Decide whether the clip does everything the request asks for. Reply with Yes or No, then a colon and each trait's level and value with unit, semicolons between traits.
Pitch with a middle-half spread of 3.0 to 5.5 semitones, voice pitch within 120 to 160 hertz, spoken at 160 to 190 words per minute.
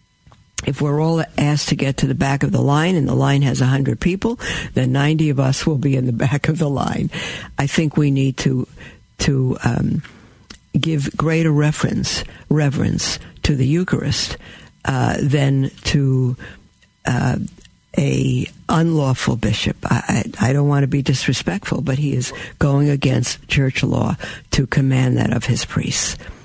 No: narrow, 2.4 semitones; medium, 140 Hz; average, 165 wpm